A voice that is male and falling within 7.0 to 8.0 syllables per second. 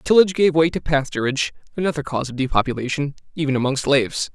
Yes: male; 7.1 syllables/s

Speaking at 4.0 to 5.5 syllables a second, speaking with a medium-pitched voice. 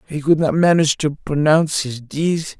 Yes: 5.1 syllables/s; medium, 155 Hz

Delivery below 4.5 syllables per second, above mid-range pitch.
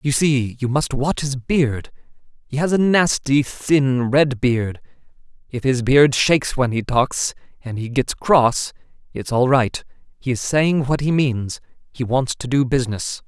No: 4.1 syllables/s; low, 135 Hz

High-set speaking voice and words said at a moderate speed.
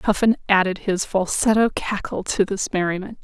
Yes: high, 195 Hz; average, 150 wpm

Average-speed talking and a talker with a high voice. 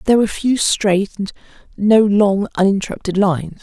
Yes: average, 150 wpm; high, 200 Hz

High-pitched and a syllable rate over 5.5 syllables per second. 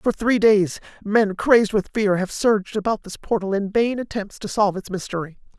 No: high, 205 Hz; 5.3 syllables/s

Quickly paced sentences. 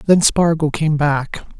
No: average, 150 wpm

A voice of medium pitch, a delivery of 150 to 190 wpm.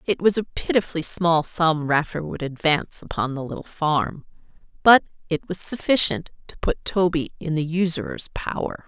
Yes: medium, 165 Hz; average, 160 wpm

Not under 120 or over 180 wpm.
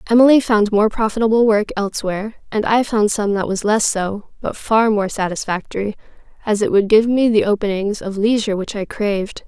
No: average, 190 wpm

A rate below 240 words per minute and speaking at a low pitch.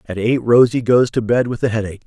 No: fast, 260 wpm; low, 115 Hz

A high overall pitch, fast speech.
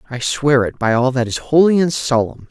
No: low, 135 Hz; fast, 240 wpm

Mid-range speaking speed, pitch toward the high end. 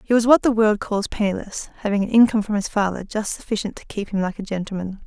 No: fast, 250 wpm; high, 205 Hz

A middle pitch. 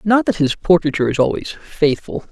Yes: medium, 165 Hz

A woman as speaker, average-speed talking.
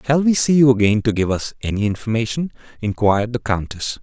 No: male; average, 195 wpm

